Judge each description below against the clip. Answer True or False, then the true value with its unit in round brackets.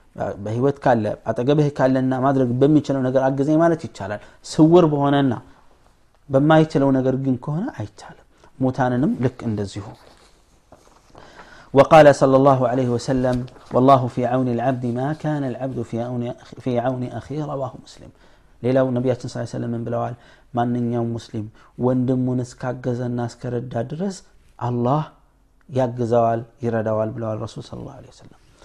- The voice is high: False (125 Hz)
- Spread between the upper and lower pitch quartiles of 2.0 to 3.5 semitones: True (2.5 semitones)